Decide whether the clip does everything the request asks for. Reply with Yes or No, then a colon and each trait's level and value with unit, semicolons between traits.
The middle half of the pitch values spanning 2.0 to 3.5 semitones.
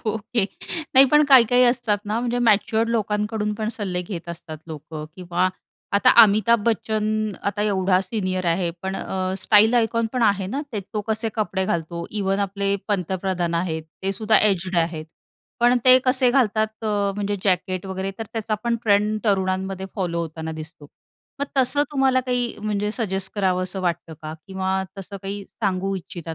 Yes: average, 3.1 semitones